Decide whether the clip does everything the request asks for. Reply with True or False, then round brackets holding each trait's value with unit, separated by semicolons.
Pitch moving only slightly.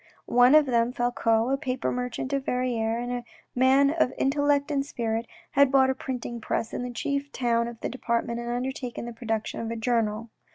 True (2.3 semitones)